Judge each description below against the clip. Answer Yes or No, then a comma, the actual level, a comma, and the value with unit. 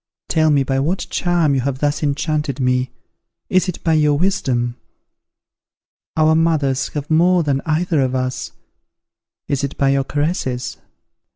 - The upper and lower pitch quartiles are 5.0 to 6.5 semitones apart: No, average, 3.2 semitones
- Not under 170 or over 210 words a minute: No, average, 150 wpm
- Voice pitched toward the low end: No, medium, 145 Hz